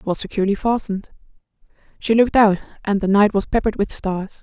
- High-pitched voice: Yes, high, 205 Hz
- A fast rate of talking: No, average, 190 wpm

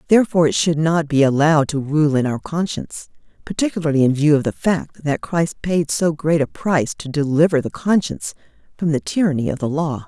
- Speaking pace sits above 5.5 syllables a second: Yes, 5.8 syllables/s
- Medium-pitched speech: Yes, medium, 155 Hz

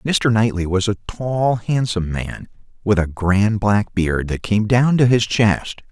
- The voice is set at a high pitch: No, low, 105 Hz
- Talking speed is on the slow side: No, average, 185 wpm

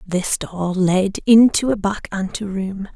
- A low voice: No, high, 195 Hz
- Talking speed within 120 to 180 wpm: Yes, average, 140 wpm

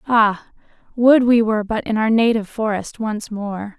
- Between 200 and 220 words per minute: No, average, 175 wpm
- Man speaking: No, female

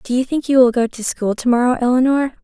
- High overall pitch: Yes, very high, 250 Hz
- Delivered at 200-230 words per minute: No, fast, 270 wpm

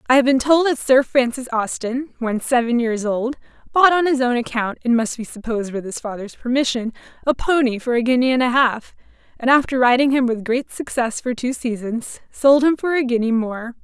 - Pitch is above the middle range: Yes, very high, 250 Hz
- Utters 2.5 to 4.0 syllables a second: No, 5.4 syllables/s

